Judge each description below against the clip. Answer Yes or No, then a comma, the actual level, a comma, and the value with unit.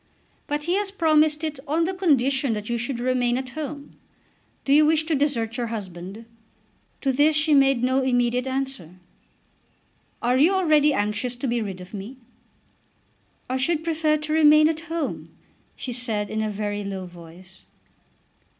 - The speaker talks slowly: No, average, 165 wpm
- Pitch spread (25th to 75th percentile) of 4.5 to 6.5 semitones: Yes, wide, 5.4 semitones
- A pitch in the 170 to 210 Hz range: No, very high, 260 Hz